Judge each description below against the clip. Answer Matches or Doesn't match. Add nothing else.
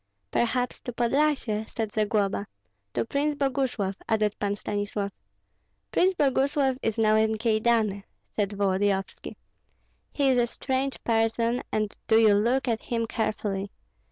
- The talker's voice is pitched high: Matches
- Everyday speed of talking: Doesn't match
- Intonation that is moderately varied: Matches